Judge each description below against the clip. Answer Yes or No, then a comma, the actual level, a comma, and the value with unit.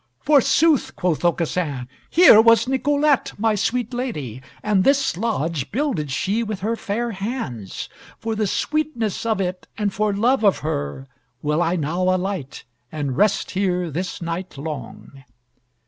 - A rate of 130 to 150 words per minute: Yes, average, 145 wpm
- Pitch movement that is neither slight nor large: No, wide, 6.0 semitones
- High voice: Yes, high, 195 Hz